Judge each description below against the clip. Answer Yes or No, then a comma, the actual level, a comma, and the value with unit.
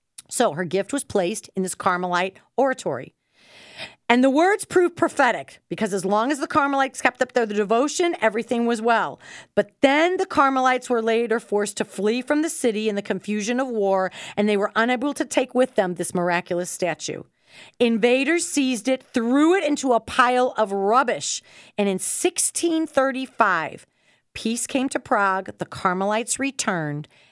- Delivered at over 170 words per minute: No, average, 165 wpm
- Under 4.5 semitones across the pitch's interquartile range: No, average, 4.9 semitones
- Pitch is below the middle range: No, high, 240 Hz